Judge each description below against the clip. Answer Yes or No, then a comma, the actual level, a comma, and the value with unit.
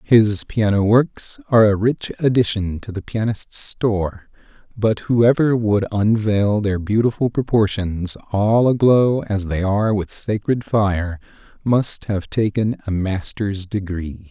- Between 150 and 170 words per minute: No, slow, 135 wpm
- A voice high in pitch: No, low, 105 Hz